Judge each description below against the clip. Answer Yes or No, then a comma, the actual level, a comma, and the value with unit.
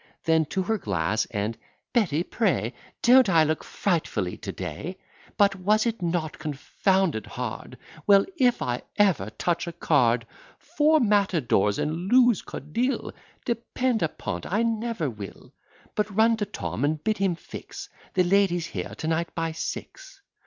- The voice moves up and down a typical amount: No, wide, 6.4 semitones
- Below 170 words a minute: Yes, average, 150 wpm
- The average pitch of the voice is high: No, medium, 180 Hz